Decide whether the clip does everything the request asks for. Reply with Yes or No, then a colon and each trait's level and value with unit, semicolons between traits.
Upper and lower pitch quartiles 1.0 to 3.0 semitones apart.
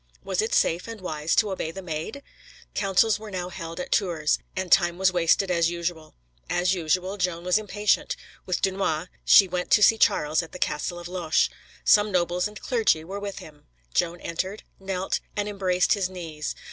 Yes: average, 2.7 semitones